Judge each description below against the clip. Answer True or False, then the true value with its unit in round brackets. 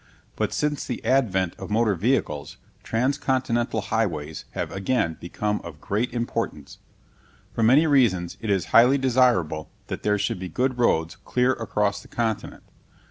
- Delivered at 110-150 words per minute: True (145 wpm)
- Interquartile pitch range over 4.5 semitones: True (5.1 semitones)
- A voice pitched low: True (115 Hz)